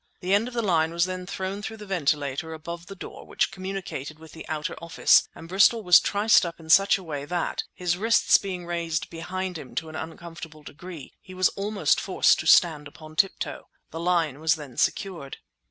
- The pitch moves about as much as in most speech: Yes, average, 3.0 semitones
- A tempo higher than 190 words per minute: Yes, average, 200 wpm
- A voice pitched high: No, medium, 170 Hz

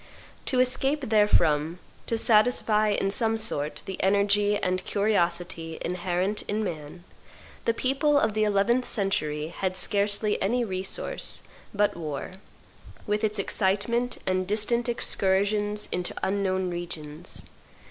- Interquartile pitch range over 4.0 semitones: No, average, 3.1 semitones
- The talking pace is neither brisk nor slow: No, slow, 120 wpm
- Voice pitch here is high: Yes, high, 200 Hz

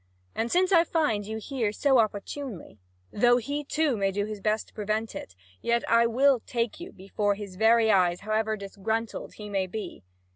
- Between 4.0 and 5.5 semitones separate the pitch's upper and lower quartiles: No, average, 3.0 semitones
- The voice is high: Yes, high, 220 Hz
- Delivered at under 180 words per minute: No, average, 185 wpm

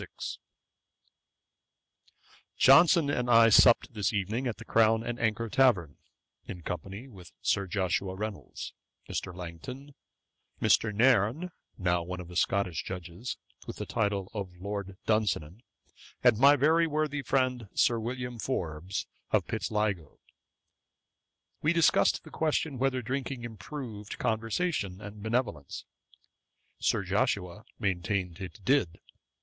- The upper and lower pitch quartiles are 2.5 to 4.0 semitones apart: No, average, 5.3 semitones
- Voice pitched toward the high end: No, low, 110 Hz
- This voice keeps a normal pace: No, slow, 120 wpm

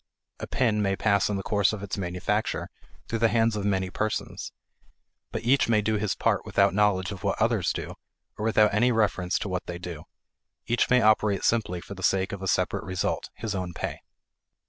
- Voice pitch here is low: Yes, low, 100 Hz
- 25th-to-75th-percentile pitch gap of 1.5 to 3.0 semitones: Yes, narrow, 2.5 semitones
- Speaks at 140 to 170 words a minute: No, fast, 205 wpm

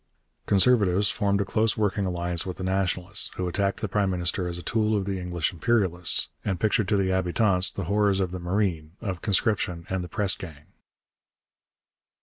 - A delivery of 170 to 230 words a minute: Yes, average, 180 wpm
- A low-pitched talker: Yes, very low, 95 Hz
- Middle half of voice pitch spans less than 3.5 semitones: Yes, narrow, 2.4 semitones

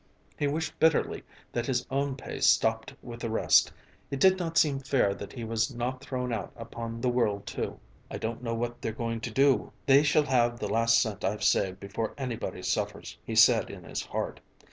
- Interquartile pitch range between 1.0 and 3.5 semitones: Yes, average, 3.2 semitones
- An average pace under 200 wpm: No, fast, 205 wpm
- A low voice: Yes, low, 120 Hz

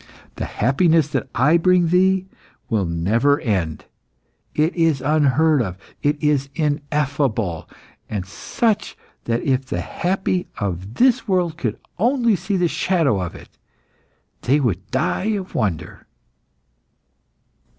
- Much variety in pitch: Yes, wide, 8.1 semitones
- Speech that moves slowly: Yes, slow, 125 wpm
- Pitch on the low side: No, medium, 145 Hz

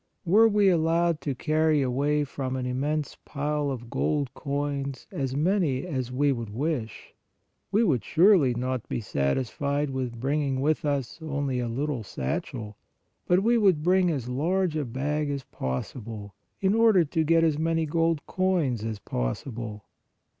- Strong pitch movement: No, average, 4.4 semitones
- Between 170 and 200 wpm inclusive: No, average, 155 wpm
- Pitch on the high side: No, medium, 145 Hz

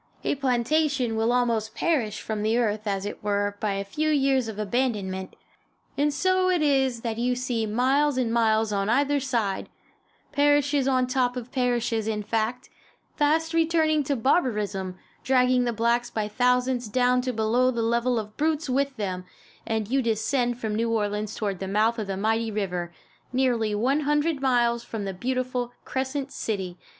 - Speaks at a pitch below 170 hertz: No, high, 240 Hz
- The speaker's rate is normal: Yes, average, 170 wpm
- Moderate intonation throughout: Yes, average, 3.6 semitones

